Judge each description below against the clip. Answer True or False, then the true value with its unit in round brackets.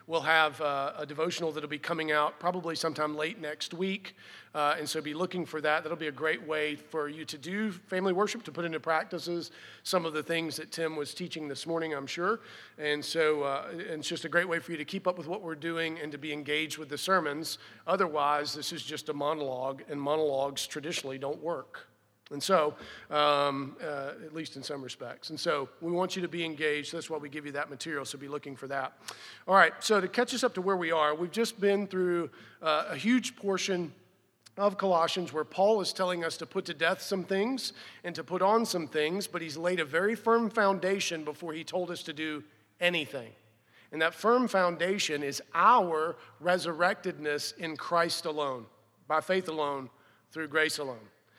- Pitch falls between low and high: True (160 Hz)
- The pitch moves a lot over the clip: False (3.2 semitones)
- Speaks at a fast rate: True (210 wpm)